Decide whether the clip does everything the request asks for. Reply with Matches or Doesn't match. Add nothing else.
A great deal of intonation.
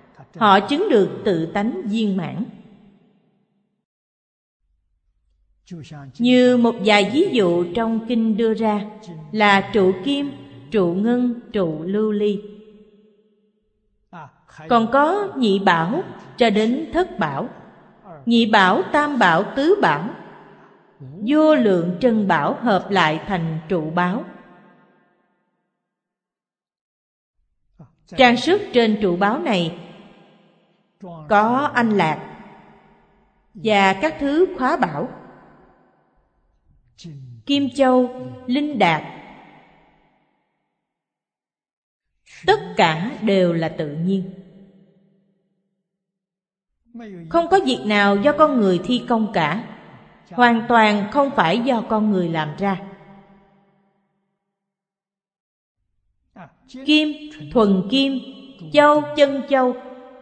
Doesn't match